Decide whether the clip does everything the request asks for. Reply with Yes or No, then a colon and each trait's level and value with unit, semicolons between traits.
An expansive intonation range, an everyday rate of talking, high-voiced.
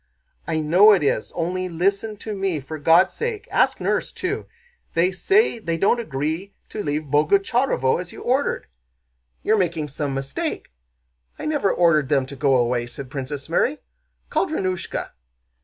No: wide, 5.9 semitones; average, 155 wpm; medium, 170 Hz